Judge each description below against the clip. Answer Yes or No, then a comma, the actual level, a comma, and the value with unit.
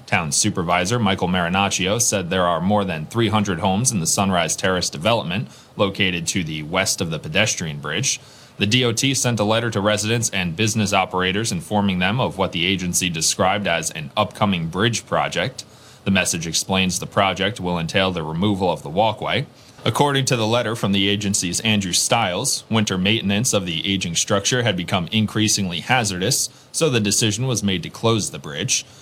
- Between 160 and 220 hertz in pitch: No, low, 100 Hz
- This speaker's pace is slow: No, average, 180 wpm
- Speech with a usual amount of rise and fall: Yes, average, 3.7 semitones